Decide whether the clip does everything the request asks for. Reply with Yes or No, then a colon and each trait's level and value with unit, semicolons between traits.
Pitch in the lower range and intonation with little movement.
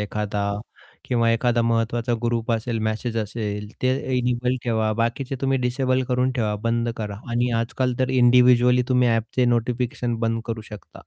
Yes: low, 120 Hz; narrow, 1.7 semitones